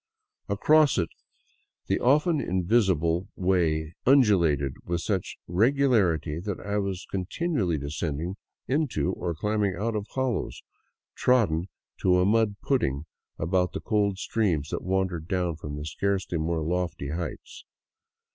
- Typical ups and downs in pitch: Yes, average, 4.5 semitones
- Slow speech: Yes, slow, 130 wpm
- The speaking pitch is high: No, very low, 95 Hz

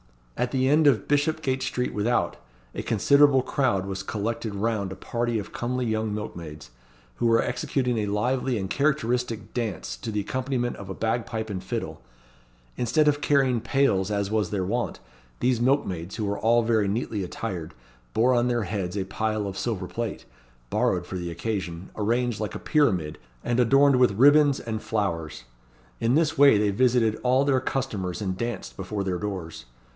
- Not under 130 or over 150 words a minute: No, average, 175 wpm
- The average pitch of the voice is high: No, low, 110 Hz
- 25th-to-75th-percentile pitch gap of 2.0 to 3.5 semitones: No, average, 4.3 semitones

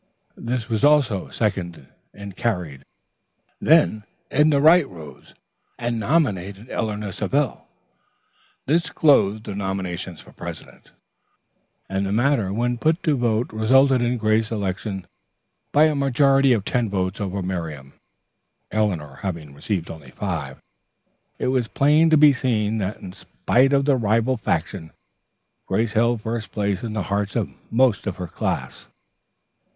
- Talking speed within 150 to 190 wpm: No, average, 140 wpm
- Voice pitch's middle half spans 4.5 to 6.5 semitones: Yes, average, 5.2 semitones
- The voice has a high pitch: No, low, 110 Hz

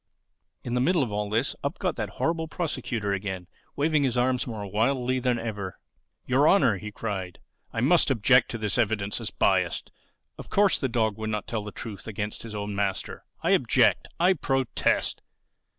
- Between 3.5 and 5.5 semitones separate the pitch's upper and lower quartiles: Yes, average, 4.4 semitones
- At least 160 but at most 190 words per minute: Yes, average, 180 wpm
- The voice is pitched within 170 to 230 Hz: No, low, 115 Hz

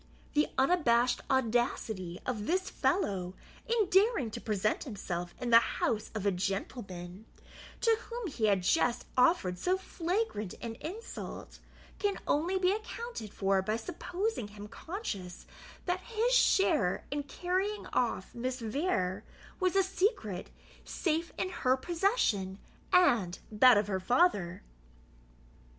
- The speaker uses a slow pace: Yes, slow, 130 wpm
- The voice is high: Yes, very high, 255 Hz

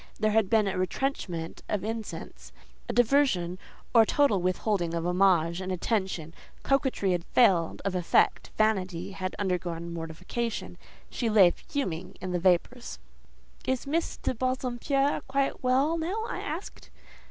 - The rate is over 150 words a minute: No, average, 140 wpm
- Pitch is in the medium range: No, high, 200 Hz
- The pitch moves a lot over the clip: Yes, wide, 6.2 semitones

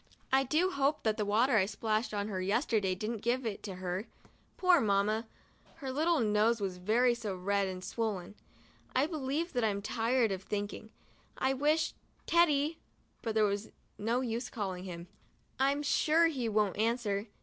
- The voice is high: Yes, high, 225 Hz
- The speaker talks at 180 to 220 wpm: No, average, 170 wpm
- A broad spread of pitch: No, average, 4.8 semitones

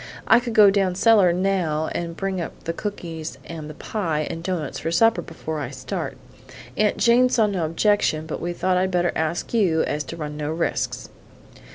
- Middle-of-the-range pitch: Yes, medium, 175 Hz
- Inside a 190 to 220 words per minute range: Yes, average, 200 wpm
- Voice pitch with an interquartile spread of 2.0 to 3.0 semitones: No, average, 4.0 semitones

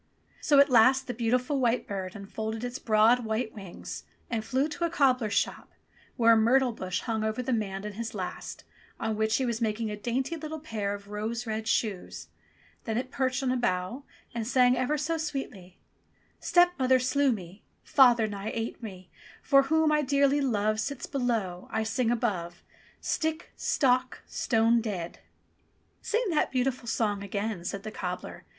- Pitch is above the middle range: Yes, high, 230 Hz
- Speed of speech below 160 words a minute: No, average, 175 wpm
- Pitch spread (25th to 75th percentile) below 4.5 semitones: Yes, average, 3.7 semitones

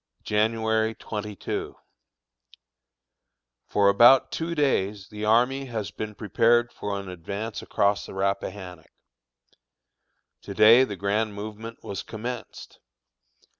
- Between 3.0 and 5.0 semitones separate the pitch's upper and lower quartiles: No, narrow, 2.4 semitones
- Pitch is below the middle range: Yes, low, 105 Hz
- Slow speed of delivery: Yes, slow, 105 wpm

